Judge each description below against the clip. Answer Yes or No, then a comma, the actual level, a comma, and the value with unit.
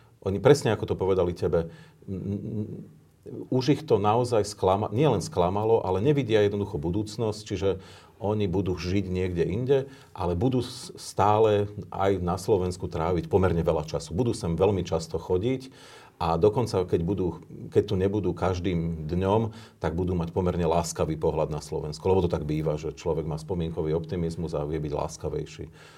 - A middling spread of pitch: Yes, average, 4.0 semitones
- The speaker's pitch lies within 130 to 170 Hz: No, very low, 95 Hz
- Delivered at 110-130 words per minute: No, fast, 165 wpm